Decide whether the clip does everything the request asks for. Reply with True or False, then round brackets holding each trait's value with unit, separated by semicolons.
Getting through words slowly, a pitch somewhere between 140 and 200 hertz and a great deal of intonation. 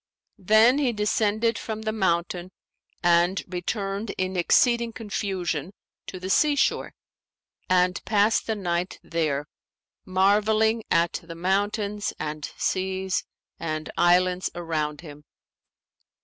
False (110 wpm; 190 Hz; 3.7 semitones)